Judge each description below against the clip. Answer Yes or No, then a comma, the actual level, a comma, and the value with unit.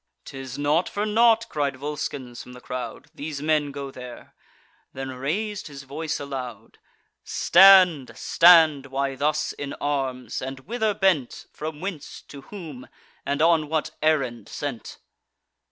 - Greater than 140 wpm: No, slow, 135 wpm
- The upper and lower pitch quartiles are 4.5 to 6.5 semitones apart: No, average, 3.4 semitones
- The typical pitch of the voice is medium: Yes, medium, 145 Hz